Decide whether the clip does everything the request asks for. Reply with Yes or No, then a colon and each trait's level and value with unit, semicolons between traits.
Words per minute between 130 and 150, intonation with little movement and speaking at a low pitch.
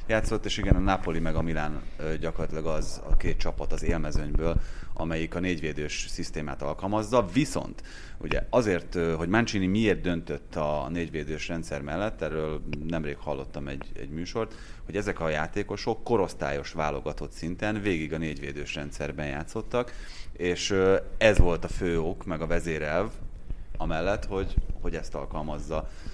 No: average, 145 wpm; average, 3.6 semitones; very low, 80 Hz